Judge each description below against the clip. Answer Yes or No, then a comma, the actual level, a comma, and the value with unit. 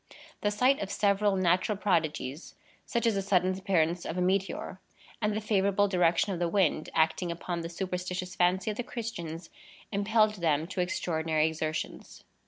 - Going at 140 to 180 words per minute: Yes, average, 165 wpm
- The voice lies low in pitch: No, medium, 185 Hz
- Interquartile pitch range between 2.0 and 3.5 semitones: Yes, average, 3.2 semitones